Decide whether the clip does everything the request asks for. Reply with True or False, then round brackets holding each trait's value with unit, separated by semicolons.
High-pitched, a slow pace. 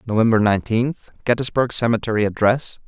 False (115 Hz; 105 wpm)